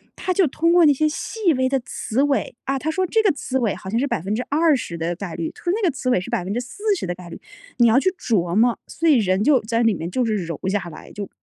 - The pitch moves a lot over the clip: Yes, wide, 8.0 semitones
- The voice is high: Yes, high, 245 Hz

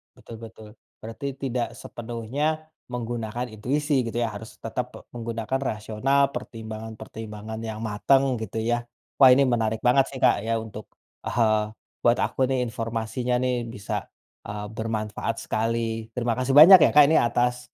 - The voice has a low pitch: Yes, low, 115 Hz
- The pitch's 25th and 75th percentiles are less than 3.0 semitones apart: Yes, narrow, 2.4 semitones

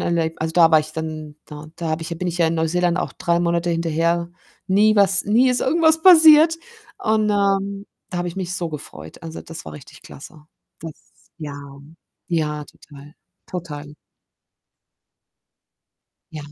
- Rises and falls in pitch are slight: No, average, 3.8 semitones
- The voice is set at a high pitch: No, medium, 170 Hz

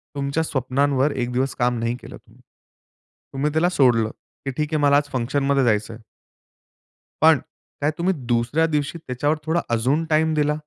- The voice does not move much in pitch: No, average, 3.6 semitones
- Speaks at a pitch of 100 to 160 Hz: Yes, medium, 140 Hz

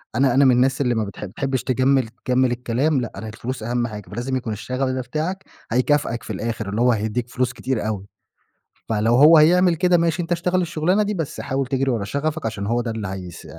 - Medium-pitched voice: No, low, 125 Hz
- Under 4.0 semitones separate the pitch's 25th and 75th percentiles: No, average, 4.6 semitones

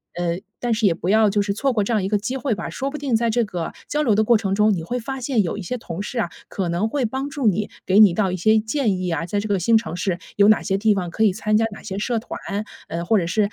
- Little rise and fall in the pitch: No, average, 3.4 semitones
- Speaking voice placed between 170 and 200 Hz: No, high, 215 Hz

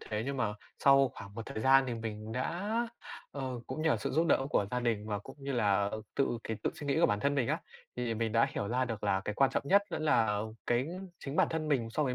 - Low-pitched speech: Yes, low, 125 Hz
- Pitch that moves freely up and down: No, average, 4.2 semitones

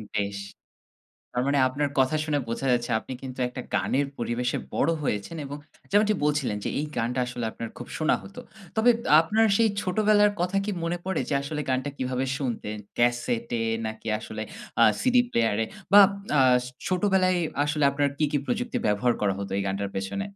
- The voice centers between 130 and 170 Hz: Yes, low, 135 Hz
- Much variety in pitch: Yes, wide, 7.3 semitones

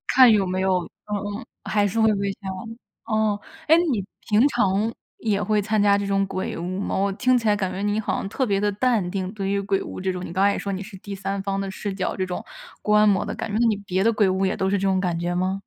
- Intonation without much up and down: Yes, narrow, 1.7 semitones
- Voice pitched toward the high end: Yes, high, 200 Hz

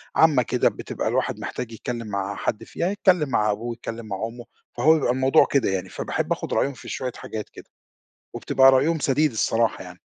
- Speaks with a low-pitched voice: Yes, low, 120 Hz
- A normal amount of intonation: Yes, average, 3.9 semitones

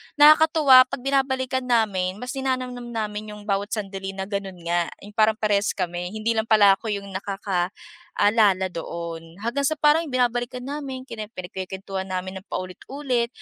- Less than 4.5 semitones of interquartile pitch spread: No, average, 5.0 semitones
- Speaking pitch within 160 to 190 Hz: No, high, 215 Hz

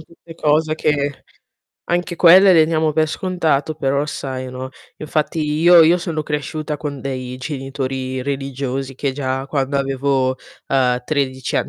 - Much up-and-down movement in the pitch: No, average, 2.9 semitones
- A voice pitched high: No, medium, 140 Hz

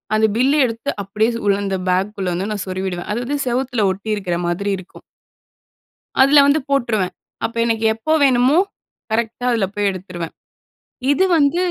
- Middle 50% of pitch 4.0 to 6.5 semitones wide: Yes, average, 4.7 semitones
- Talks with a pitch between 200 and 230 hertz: Yes, high, 220 Hz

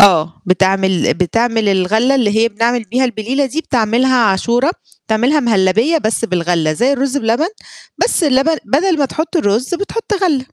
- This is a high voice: Yes, high, 235 Hz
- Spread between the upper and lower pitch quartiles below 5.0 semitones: No, average, 5.3 semitones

